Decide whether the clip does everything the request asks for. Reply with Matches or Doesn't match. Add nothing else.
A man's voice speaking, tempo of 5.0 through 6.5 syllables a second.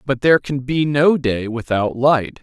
Doesn't match